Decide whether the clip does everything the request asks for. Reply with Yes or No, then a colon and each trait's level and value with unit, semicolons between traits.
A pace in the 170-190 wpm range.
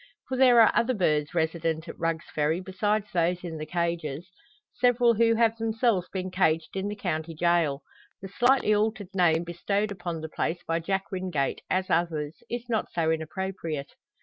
Yes: average, 175 wpm